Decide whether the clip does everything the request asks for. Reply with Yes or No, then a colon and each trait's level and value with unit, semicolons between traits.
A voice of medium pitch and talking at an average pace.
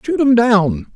No: high, 220 Hz; average, 190 wpm